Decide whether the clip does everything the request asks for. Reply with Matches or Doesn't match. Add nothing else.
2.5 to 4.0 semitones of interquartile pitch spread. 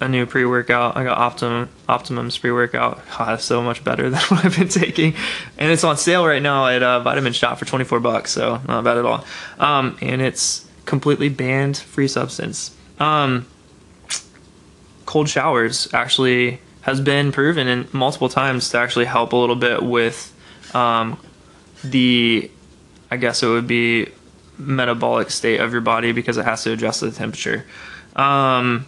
Matches